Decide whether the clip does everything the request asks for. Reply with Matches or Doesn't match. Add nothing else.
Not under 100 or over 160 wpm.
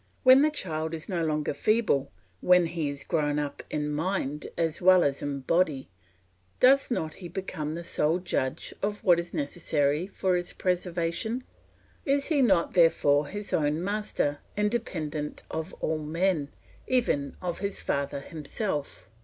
Matches